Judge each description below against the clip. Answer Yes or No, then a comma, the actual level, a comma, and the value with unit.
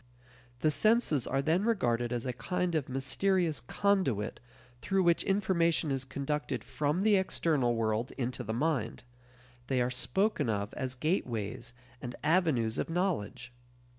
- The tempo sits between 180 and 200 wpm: No, average, 140 wpm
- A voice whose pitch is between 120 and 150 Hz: Yes, medium, 140 Hz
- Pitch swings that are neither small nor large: No, wide, 6.6 semitones